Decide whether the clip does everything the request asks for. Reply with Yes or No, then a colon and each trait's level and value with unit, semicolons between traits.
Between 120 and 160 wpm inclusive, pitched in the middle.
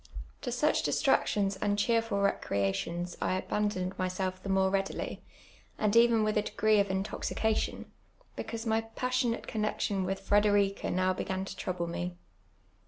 No: average, 145 wpm; high, 200 Hz